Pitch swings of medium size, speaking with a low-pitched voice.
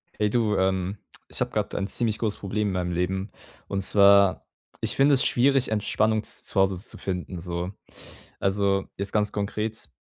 No: narrow, 2.3 semitones; low, 100 Hz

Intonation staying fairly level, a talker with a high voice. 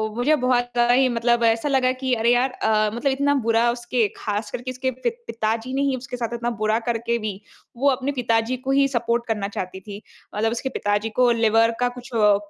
Yes: narrow, 2.3 semitones; high, 240 Hz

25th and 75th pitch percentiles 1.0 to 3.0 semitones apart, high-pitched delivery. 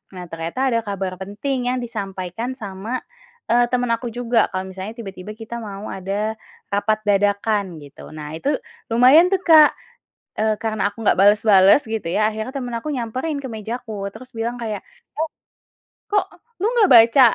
No: average, 3.7 semitones; high, 220 Hz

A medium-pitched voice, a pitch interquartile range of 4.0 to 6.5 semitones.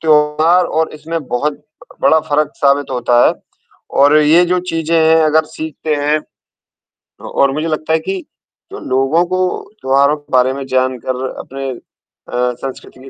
No: medium, 150 Hz; average, 2.9 semitones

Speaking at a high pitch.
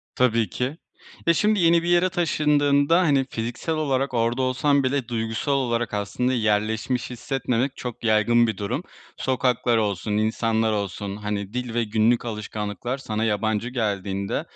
No: low, 120 Hz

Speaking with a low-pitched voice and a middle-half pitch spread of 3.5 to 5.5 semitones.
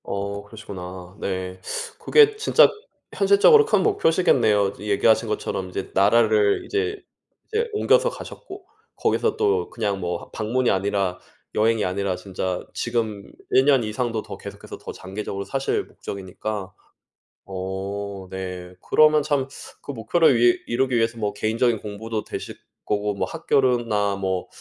Yes: low, 110 Hz; average, 5.2 semitones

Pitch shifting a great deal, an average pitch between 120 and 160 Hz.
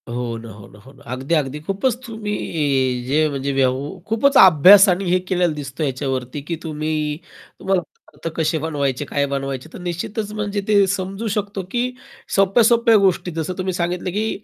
No: wide, 6.1 semitones; medium, 170 Hz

